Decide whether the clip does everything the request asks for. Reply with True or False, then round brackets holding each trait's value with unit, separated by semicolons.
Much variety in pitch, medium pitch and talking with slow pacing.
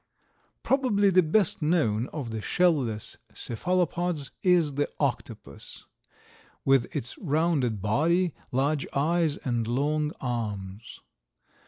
True (6.3 semitones; 145 Hz; 110 wpm)